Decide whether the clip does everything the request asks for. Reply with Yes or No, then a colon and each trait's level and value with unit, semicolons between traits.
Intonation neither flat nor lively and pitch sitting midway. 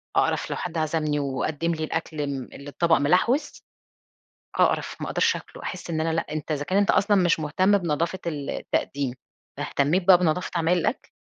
Yes: average, 3.3 semitones; medium, 160 Hz